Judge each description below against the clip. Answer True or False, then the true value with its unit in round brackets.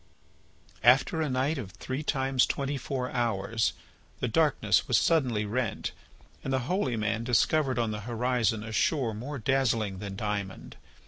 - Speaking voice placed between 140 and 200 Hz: False (120 Hz)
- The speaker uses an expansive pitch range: False (3.8 semitones)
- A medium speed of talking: True (150 wpm)